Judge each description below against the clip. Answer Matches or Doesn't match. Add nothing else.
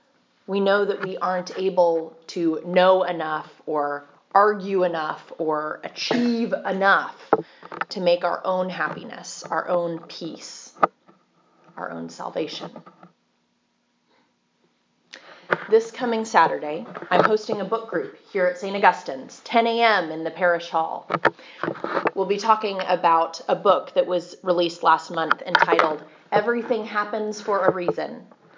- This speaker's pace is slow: Matches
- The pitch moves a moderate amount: Matches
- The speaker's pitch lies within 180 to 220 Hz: Matches